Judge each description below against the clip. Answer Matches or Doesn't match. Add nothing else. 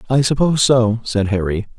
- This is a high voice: Doesn't match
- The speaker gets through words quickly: Doesn't match